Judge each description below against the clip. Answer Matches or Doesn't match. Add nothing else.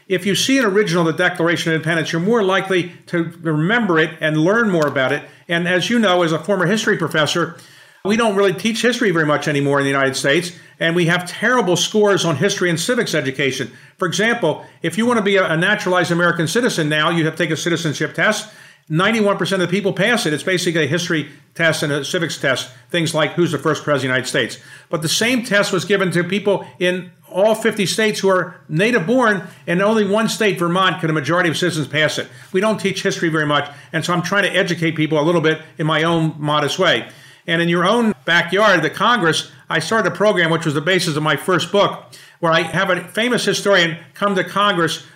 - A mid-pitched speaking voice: Matches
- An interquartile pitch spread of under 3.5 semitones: Doesn't match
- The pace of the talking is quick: Matches